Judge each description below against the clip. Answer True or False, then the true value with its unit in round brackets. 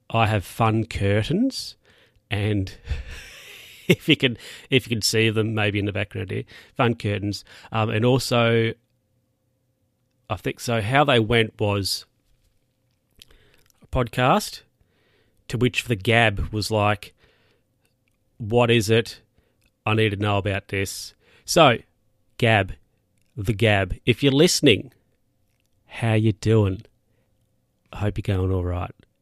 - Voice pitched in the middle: False (110 Hz)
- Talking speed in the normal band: False (130 wpm)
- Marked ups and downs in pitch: False (3.0 semitones)